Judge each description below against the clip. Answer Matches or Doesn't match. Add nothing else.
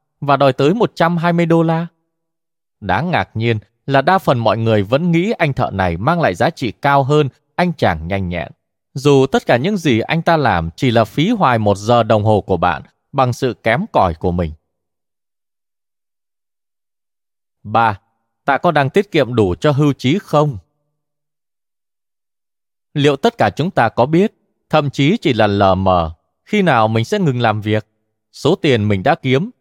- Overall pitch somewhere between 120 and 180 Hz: Matches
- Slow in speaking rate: Doesn't match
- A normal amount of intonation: Doesn't match